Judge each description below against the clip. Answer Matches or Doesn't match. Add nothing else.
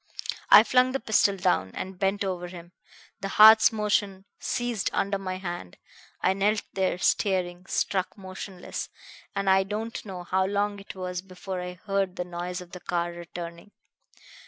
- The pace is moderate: Matches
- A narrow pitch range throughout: Matches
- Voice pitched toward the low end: Doesn't match